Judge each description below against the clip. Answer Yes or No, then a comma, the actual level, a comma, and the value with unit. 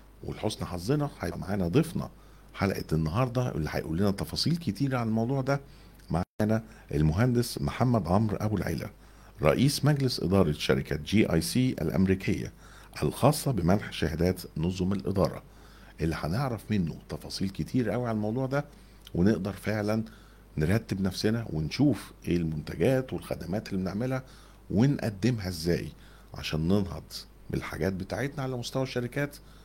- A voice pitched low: Yes, low, 105 Hz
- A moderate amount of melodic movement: No, wide, 6.4 semitones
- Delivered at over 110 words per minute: Yes, average, 125 wpm